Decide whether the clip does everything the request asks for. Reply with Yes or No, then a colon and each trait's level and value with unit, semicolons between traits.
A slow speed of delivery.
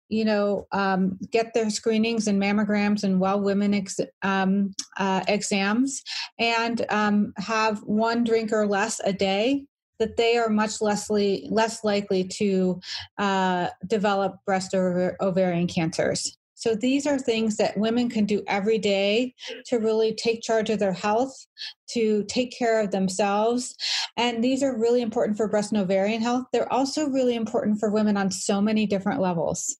No: average, 165 wpm